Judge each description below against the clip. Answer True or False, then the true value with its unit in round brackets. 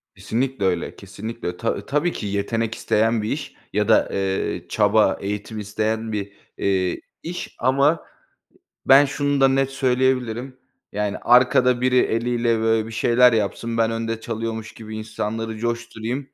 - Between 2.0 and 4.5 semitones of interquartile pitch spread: True (2.8 semitones)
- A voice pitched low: True (115 Hz)